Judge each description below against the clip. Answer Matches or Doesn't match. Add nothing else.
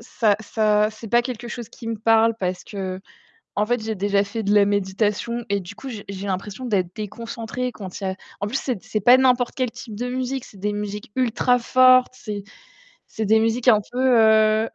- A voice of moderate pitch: Doesn't match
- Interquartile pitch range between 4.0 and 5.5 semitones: Doesn't match